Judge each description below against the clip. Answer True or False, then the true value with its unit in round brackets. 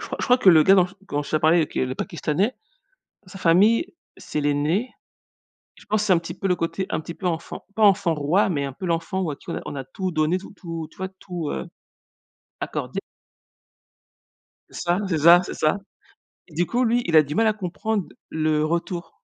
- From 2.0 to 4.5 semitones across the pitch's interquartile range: True (3.7 semitones)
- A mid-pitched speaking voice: True (170 Hz)